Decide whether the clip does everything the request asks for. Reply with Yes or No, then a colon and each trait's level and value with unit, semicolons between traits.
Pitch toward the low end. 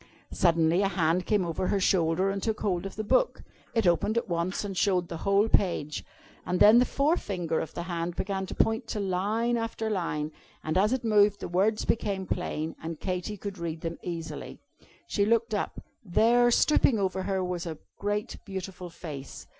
No: high, 190 Hz